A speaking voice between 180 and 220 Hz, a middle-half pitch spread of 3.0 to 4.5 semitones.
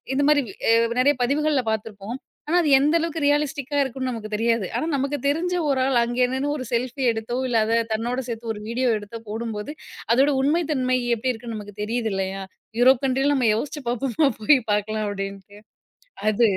No: high, 245 Hz; average, 4.1 semitones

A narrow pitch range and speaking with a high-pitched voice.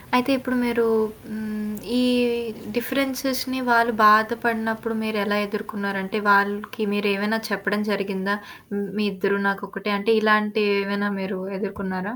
Yes: narrow, 2.0 semitones; high, 210 Hz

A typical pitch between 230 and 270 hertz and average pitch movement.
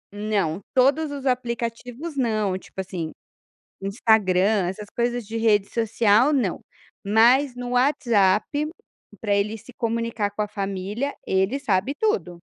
No: high, 220 Hz; average, 3.8 semitones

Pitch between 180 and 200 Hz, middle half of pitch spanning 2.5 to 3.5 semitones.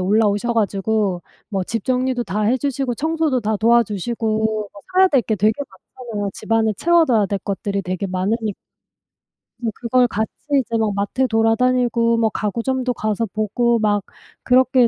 No: high, 225 Hz; average, 3.2 semitones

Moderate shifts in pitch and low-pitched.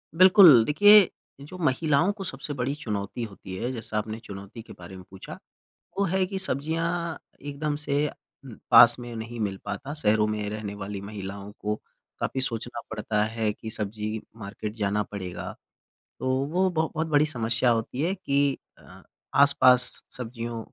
No: wide, 5.8 semitones; low, 120 Hz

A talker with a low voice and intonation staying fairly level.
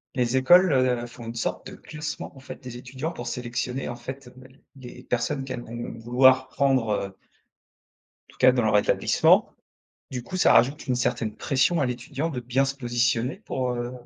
Yes: low, 125 Hz; narrow, 1.9 semitones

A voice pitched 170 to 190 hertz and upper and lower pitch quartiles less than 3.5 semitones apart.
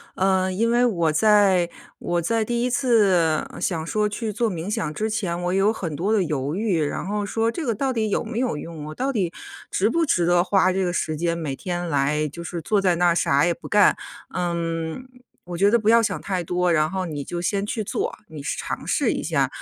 No: medium, 185 Hz; average, 4.3 semitones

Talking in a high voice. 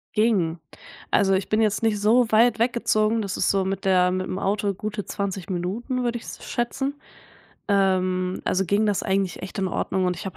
Yes: high, 200 Hz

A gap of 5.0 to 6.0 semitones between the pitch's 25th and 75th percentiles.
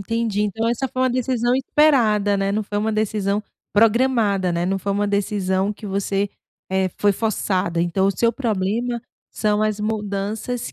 No: narrow, 2.6 semitones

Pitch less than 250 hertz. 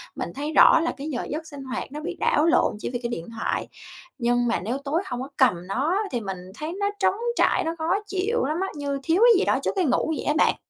No: very high, 290 Hz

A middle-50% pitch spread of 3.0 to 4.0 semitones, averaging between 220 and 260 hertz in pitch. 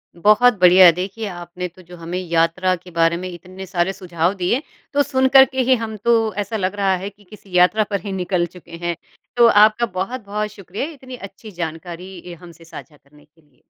No: average, 3.6 semitones; medium, 185 Hz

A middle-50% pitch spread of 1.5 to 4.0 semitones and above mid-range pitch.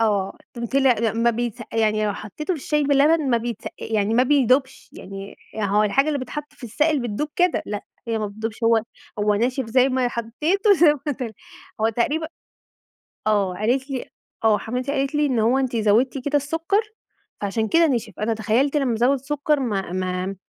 No: average, 4.5 semitones; high, 240 Hz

